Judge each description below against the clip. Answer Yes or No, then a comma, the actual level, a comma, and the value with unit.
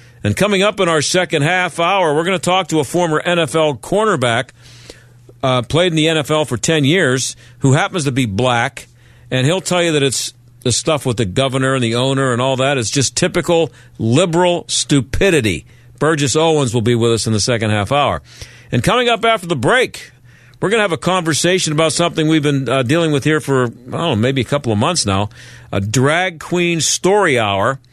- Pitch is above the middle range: No, medium, 140 Hz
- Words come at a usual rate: No, fast, 210 wpm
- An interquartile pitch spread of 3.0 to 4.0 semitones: No, wide, 5.4 semitones